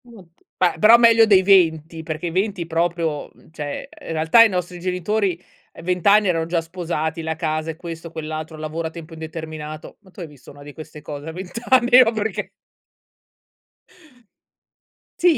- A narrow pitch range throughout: No, average, 3.1 semitones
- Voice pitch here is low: No, medium, 165 Hz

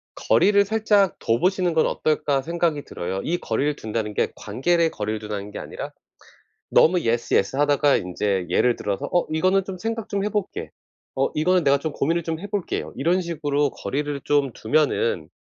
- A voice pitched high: No, medium, 150 Hz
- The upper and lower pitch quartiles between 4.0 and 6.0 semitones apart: No, wide, 7.4 semitones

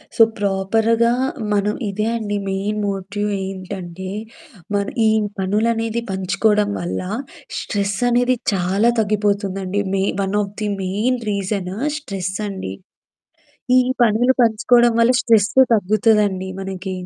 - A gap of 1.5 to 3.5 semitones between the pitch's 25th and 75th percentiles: Yes, narrow, 2.4 semitones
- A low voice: No, high, 205 Hz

